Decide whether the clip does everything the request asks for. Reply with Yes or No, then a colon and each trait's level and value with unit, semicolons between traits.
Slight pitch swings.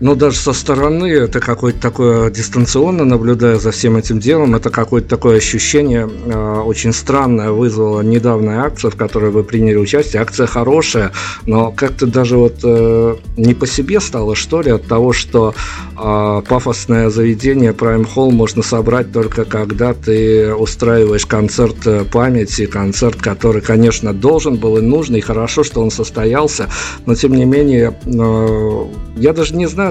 Yes: narrow, 2.0 semitones